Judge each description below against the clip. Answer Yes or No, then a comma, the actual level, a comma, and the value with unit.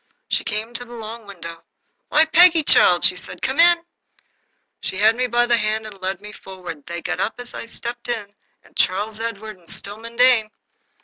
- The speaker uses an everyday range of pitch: Yes, average, 3.5 semitones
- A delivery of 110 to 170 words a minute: No, average, 190 wpm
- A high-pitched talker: Yes, high, 220 Hz